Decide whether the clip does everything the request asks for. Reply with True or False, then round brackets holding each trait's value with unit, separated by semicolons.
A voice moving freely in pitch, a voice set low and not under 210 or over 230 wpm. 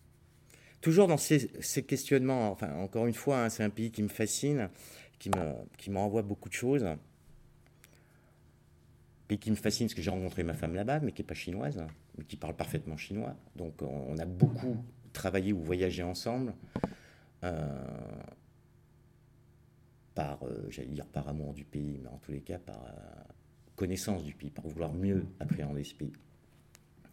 False (6.9 semitones; 95 Hz; 175 wpm)